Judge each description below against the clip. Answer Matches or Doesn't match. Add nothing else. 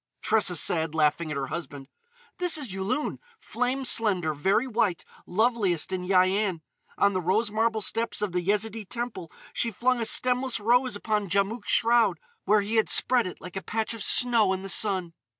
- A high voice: Matches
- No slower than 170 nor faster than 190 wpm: Matches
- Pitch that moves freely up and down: Doesn't match